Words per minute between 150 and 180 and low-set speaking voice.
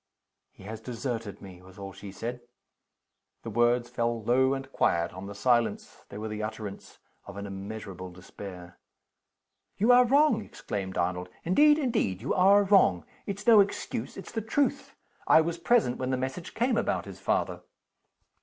Yes: average, 165 wpm; low, 120 Hz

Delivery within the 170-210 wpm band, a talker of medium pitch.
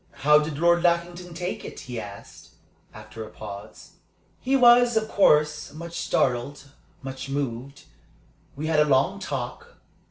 No: average, 140 wpm; medium, 150 Hz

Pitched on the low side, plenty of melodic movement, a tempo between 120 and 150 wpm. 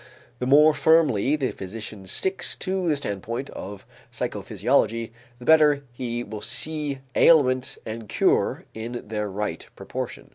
Yes: low, 125 Hz; wide, 5.7 semitones; slow, 135 wpm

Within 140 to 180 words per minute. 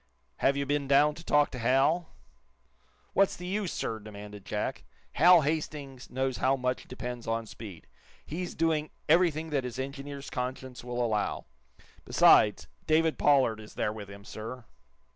Yes: average, 155 wpm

